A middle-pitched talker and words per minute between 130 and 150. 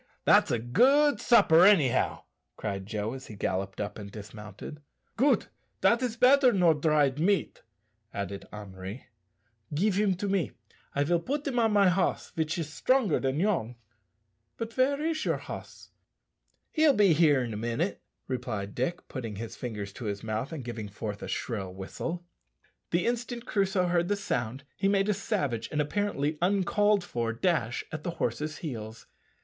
No: medium, 155 Hz; average, 165 wpm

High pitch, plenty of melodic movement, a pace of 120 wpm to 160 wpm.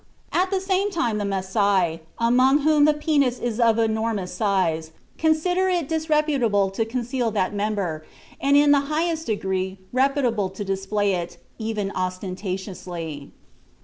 Yes: high, 220 Hz; wide, 7.0 semitones; average, 140 wpm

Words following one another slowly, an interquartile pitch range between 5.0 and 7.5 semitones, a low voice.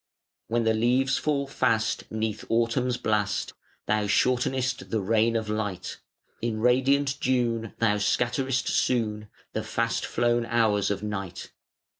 No: slow, 130 wpm; average, 2.8 semitones; low, 115 Hz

